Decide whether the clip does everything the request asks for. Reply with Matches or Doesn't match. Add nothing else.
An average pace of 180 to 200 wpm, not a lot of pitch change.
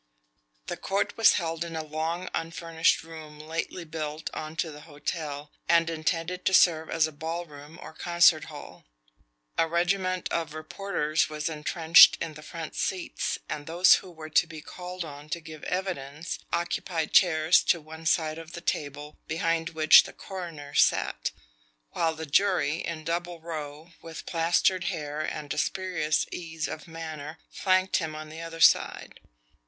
Doesn't match